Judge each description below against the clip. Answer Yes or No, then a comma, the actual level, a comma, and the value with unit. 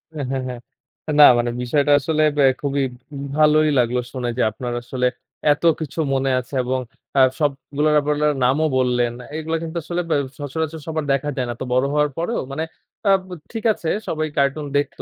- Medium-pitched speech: Yes, medium, 145 Hz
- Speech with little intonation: No, average, 3.2 semitones